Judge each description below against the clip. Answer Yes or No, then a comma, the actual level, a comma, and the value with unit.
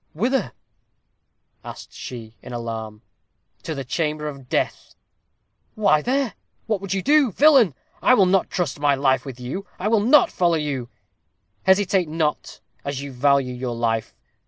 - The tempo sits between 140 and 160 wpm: Yes, average, 155 wpm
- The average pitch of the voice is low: No, medium, 150 Hz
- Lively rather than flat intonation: Yes, wide, 7.4 semitones